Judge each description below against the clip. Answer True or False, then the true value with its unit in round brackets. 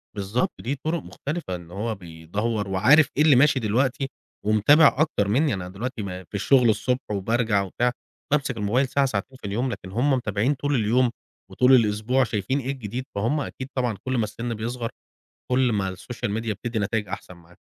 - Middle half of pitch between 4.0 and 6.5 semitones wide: True (4.4 semitones)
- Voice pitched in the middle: False (115 Hz)